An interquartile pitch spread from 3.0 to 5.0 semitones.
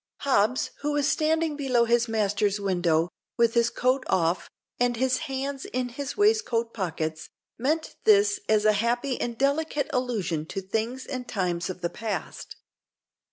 No: wide, 5.4 semitones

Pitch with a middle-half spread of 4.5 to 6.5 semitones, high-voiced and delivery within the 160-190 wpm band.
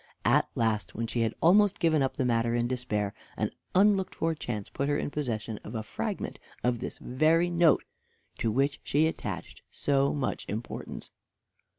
No: wide, 5.5 semitones; low, 130 Hz; average, 175 wpm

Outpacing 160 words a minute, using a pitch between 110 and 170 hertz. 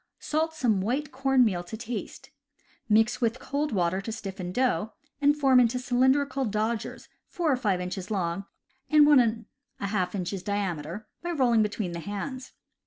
No: average, 175 wpm; high, 225 Hz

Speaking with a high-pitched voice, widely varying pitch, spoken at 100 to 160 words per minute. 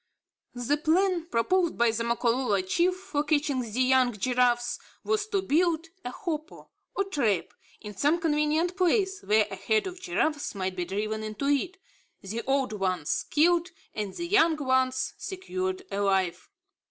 Yes: very high, 285 Hz; wide, 7.6 semitones; average, 155 wpm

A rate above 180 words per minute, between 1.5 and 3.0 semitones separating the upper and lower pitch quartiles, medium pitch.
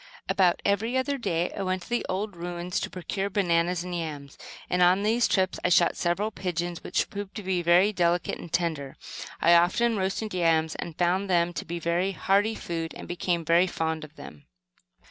Yes: average, 195 wpm; narrow, 2.4 semitones; medium, 180 Hz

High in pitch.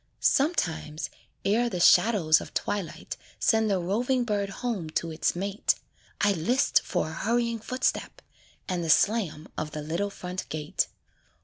Yes: high, 195 Hz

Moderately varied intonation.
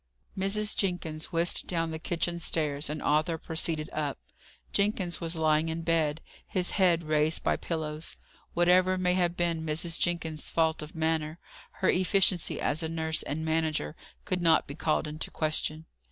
No: narrow, 1.9 semitones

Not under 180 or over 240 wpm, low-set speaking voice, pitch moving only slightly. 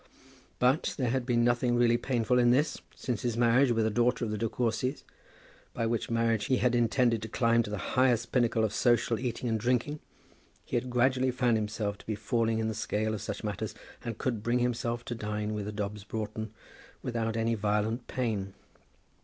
Yes: average, 200 wpm; low, 115 Hz; narrow, 2.0 semitones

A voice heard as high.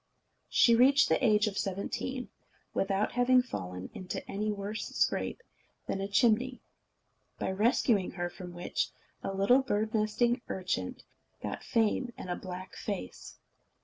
Yes: high, 210 Hz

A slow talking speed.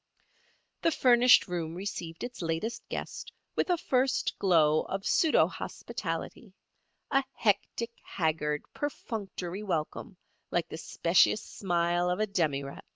Yes: slow, 120 wpm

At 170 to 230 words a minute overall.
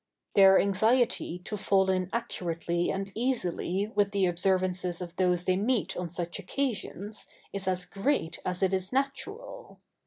No: average, 155 wpm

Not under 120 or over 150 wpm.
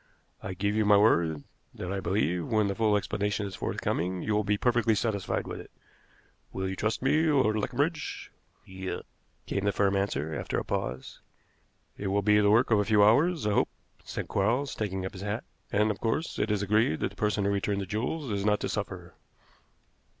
No: fast, 205 wpm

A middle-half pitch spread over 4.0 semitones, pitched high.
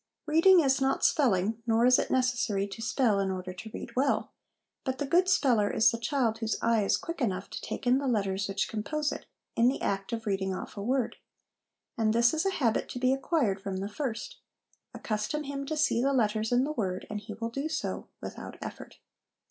Yes: average, 4.7 semitones; high, 235 Hz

